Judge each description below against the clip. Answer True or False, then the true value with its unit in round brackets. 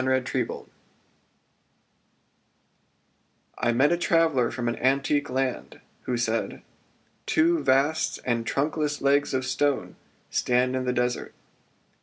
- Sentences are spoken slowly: True (110 wpm)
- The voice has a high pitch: False (130 Hz)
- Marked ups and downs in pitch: False (2.6 semitones)